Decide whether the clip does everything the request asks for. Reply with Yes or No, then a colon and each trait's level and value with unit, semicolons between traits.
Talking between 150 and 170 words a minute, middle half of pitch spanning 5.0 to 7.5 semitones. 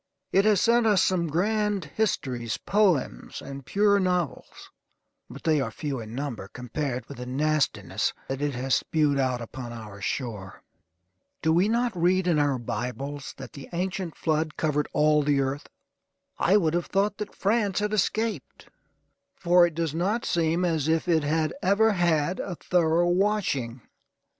Yes: average, 160 wpm; wide, 5.6 semitones